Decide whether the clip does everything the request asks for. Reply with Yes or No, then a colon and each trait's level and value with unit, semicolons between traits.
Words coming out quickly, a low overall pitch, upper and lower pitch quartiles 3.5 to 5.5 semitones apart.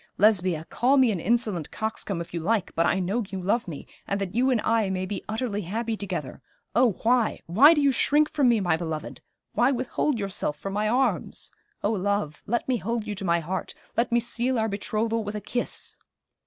No: fast, 210 wpm; high, 215 Hz; average, 4.2 semitones